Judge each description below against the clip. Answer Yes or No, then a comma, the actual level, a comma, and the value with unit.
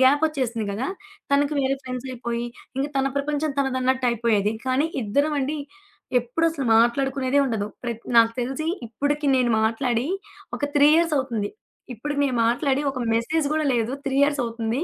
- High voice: Yes, very high, 260 Hz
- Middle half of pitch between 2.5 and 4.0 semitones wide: Yes, average, 3.4 semitones